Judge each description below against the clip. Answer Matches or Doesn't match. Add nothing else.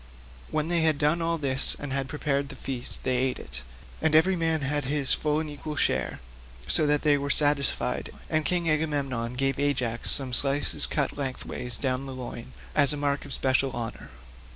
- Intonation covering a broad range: Doesn't match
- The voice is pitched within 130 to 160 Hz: Matches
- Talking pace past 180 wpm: Matches